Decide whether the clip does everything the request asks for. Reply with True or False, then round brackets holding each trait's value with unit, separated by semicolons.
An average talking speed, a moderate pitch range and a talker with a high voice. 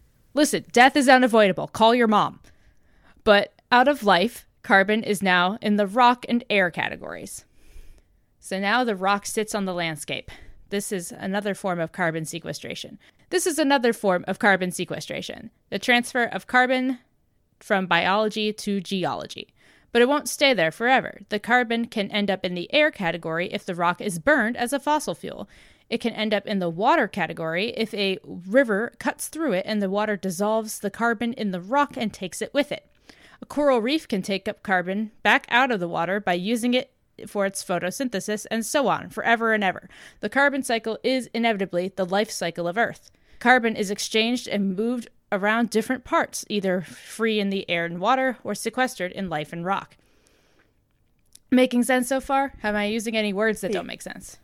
True (185 wpm; 4.1 semitones; 210 Hz)